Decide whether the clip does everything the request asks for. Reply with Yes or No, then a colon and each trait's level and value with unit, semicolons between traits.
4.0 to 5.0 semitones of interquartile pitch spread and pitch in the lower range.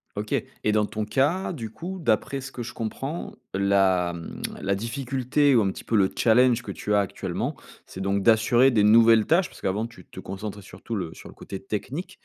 Yes: average, 4.6 semitones; low, 110 Hz